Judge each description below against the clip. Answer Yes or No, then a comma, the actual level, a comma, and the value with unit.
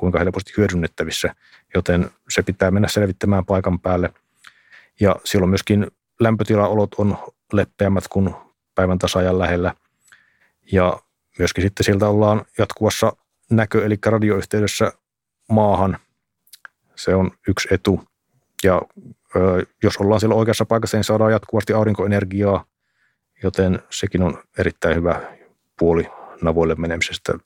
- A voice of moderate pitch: No, low, 100 Hz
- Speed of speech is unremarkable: Yes, average, 115 wpm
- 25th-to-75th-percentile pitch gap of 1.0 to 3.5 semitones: Yes, average, 2.7 semitones